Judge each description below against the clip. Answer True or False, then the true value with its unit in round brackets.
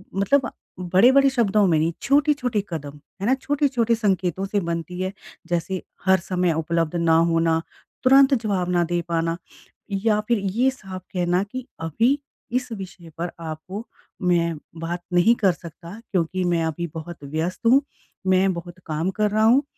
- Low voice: False (185 Hz)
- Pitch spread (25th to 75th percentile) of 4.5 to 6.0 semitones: True (4.9 semitones)